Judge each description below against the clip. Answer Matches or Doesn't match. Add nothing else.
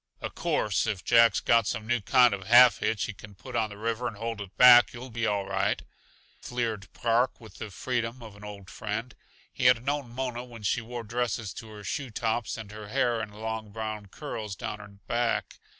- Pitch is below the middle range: Matches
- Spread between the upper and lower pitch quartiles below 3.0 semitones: Matches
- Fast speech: Matches